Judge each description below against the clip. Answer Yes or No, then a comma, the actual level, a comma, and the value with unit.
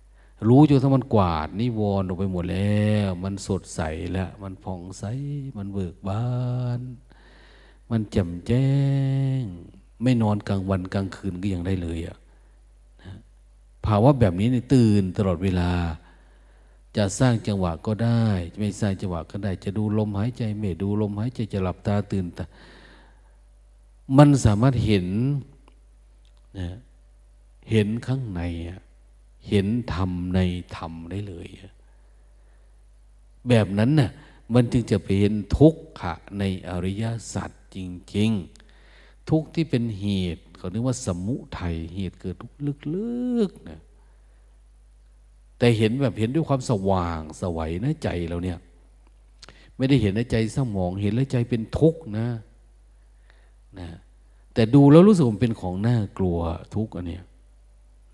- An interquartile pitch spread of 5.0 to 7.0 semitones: Yes, wide, 5.4 semitones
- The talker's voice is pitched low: Yes, low, 100 Hz